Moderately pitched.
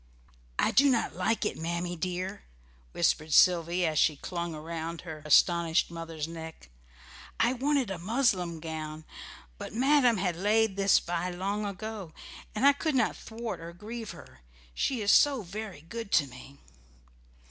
Yes: medium, 180 Hz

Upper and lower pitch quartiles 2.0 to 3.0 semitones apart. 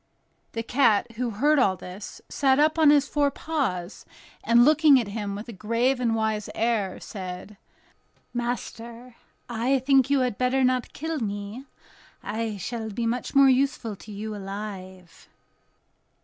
No: average, 4.3 semitones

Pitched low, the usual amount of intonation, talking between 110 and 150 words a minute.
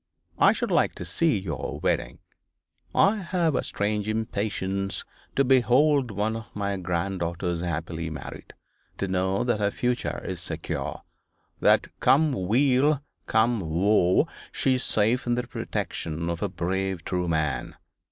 No: low, 100 Hz; wide, 5.8 semitones; average, 140 wpm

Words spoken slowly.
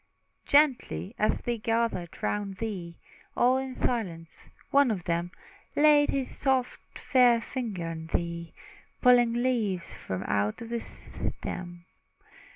Yes: slow, 120 wpm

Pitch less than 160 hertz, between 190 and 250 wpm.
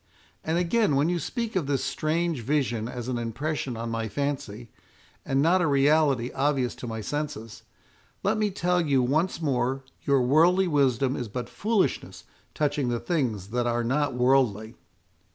No: medium, 140 Hz; average, 165 wpm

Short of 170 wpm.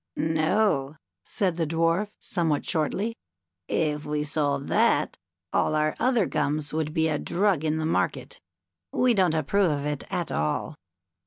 Yes: average, 150 wpm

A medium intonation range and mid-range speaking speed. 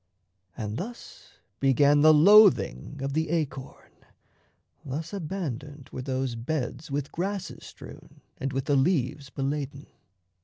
No: average, 3.1 semitones; slow, 120 wpm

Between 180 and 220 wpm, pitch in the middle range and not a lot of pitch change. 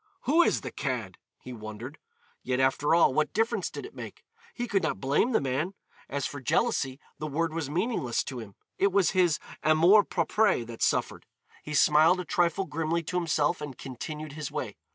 No: average, 190 wpm; medium, 155 Hz; average, 5.3 semitones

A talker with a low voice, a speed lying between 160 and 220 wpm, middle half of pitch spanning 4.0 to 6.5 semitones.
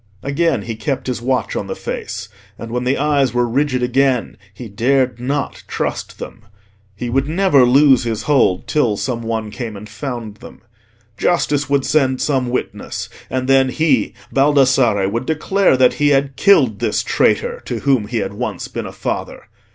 No: low, 130 Hz; average, 175 wpm; average, 3.2 semitones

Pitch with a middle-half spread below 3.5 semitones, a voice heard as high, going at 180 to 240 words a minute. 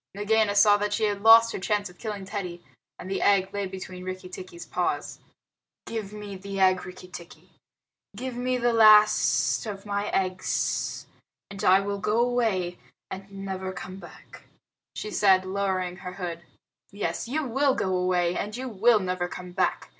No: narrow, 2.4 semitones; high, 195 Hz; average, 170 wpm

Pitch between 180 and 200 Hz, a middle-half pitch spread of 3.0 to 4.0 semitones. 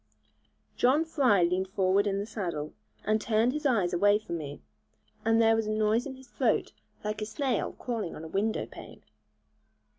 No: high, 215 Hz; average, 3.5 semitones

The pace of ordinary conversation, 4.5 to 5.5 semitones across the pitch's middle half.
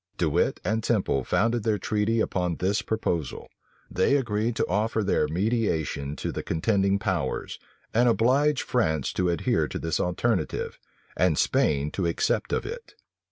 Yes: average, 155 wpm; average, 5.1 semitones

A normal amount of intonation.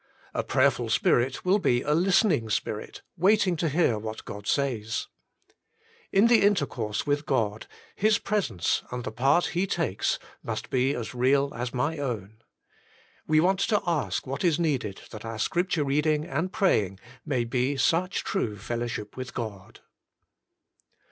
No: wide, 7.0 semitones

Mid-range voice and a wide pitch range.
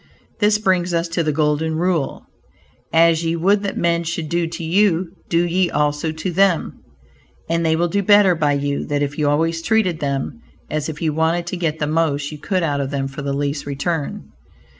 No: medium, 165 Hz; average, 2.8 semitones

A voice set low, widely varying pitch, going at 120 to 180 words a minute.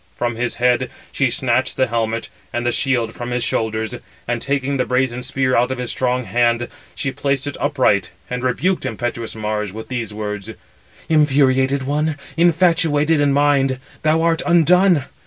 No: low, 130 Hz; average, 3.3 semitones; average, 165 wpm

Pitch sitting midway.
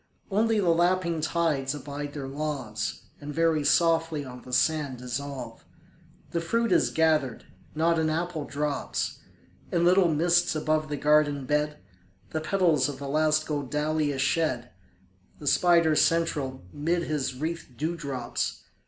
Yes: medium, 150 Hz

